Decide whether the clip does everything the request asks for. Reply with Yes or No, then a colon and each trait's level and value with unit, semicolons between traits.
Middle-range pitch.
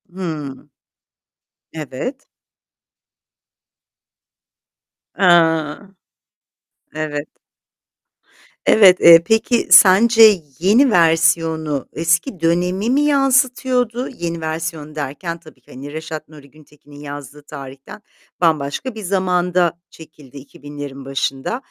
Yes: medium, 165 Hz